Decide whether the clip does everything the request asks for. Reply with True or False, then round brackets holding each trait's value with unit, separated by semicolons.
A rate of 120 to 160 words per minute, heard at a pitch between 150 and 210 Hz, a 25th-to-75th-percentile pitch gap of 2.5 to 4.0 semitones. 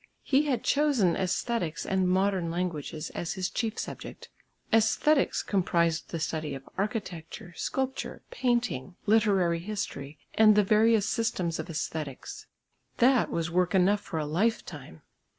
False (135 wpm; 190 Hz; 5.1 semitones)